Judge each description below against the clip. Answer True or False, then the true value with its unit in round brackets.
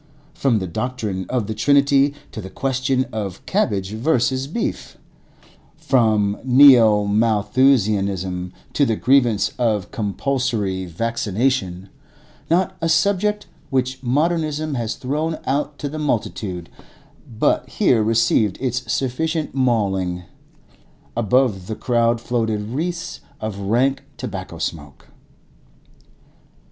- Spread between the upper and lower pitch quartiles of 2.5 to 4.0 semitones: False (4.8 semitones)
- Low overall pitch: True (120 Hz)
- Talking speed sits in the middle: False (110 wpm)